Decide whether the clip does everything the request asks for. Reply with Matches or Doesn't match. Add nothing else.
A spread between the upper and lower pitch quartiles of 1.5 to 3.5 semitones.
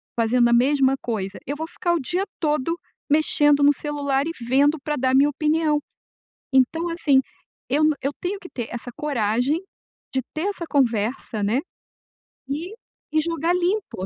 Doesn't match